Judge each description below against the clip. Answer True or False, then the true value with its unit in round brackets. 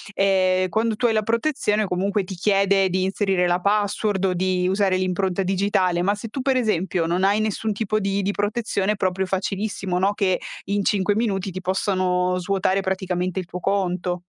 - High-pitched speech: True (195 Hz)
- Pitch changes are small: True (1.9 semitones)